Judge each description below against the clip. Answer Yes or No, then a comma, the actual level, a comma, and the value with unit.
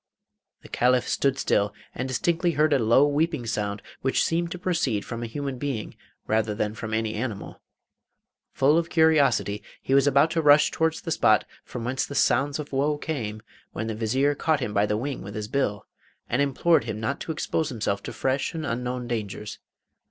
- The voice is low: Yes, low, 130 Hz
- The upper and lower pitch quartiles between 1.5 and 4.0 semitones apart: No, average, 5.0 semitones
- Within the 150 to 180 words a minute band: No, average, 195 wpm